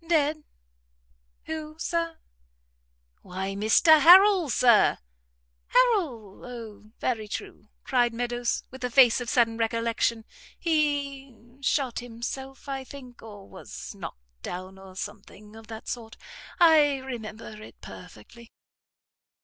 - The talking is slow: Yes, slow, 115 wpm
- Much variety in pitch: No, average, 4.5 semitones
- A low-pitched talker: No, high, 240 Hz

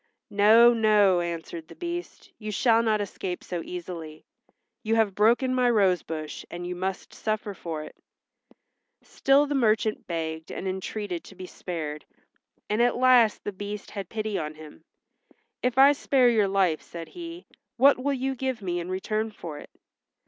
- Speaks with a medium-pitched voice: No, high, 205 Hz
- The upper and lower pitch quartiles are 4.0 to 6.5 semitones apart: Yes, average, 5.2 semitones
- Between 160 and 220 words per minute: Yes, average, 170 wpm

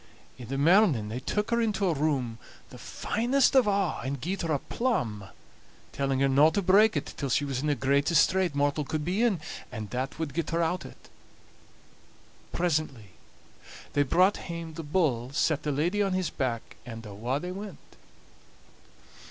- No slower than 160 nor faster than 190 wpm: Yes, average, 180 wpm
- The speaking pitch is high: No, medium, 155 Hz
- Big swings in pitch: Yes, wide, 5.7 semitones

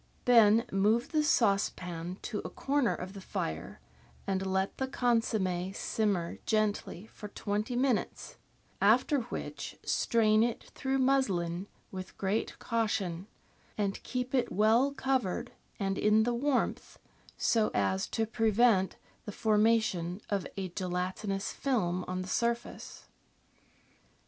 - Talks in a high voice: Yes, high, 210 Hz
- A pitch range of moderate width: Yes, average, 4.0 semitones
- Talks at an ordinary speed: No, slow, 125 wpm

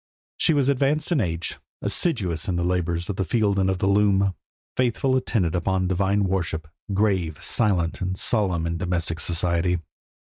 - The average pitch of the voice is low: Yes, very low, 95 Hz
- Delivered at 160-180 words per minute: Yes, average, 170 wpm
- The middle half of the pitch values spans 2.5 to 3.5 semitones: Yes, average, 3.2 semitones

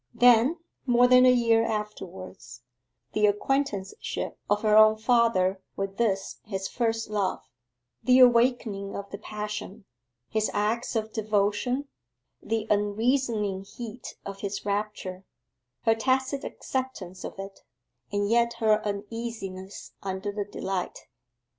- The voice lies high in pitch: Yes, high, 215 Hz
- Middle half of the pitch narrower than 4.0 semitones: Yes, average, 2.9 semitones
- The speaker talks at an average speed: No, slow, 120 wpm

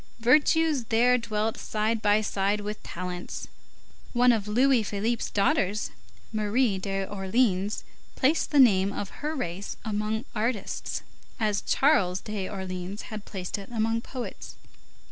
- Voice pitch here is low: No, high, 215 Hz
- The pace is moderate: No, slow, 125 wpm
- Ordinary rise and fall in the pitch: Yes, average, 3.4 semitones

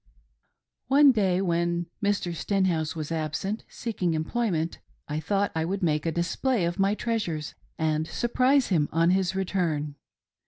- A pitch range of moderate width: Yes, average, 4.1 semitones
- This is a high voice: No, medium, 175 Hz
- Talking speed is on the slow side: No, average, 150 wpm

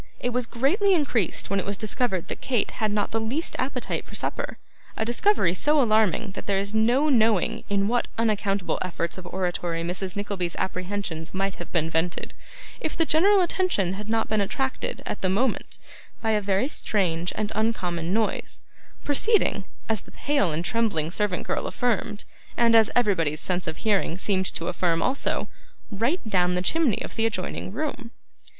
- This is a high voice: Yes, high, 210 Hz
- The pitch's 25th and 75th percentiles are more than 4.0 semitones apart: Yes, average, 4.6 semitones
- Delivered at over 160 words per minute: Yes, average, 175 wpm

